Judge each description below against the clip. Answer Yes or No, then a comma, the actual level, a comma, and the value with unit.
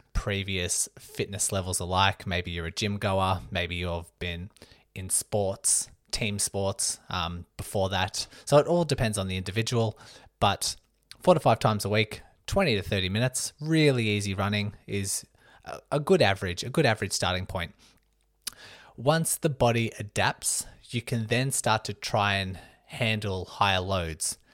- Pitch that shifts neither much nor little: Yes, average, 3.7 semitones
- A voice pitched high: No, low, 100 Hz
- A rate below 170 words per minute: Yes, average, 155 wpm